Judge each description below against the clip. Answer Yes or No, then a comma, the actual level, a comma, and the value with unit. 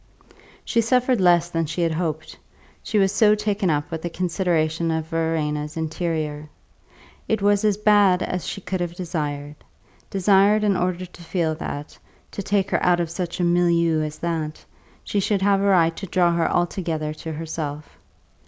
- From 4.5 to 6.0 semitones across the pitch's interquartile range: No, average, 3.3 semitones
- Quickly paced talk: No, average, 175 wpm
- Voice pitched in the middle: Yes, medium, 175 Hz